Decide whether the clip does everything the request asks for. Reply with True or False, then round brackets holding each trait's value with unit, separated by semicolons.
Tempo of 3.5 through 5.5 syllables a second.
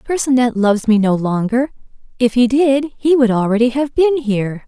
True (5.2 syllables/s)